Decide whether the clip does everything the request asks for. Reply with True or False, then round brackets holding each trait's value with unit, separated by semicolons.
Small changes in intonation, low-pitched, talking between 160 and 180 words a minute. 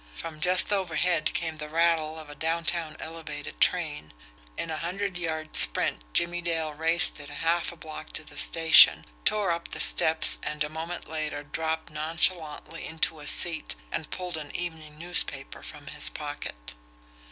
False (1.9 semitones; 160 Hz; 165 wpm)